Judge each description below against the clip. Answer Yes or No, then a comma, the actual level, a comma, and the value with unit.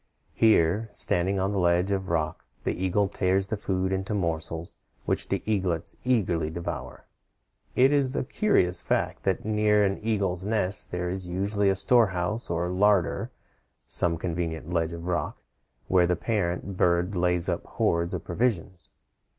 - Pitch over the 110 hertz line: No, very low, 95 Hz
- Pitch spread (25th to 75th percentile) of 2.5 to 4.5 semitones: Yes, average, 2.9 semitones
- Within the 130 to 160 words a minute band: Yes, average, 155 wpm